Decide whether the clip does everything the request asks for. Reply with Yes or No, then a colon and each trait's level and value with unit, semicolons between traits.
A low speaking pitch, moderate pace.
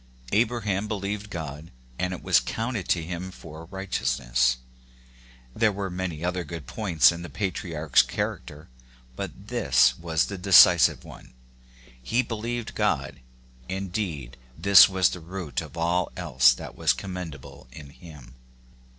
Yes: very low, 85 Hz; average, 150 wpm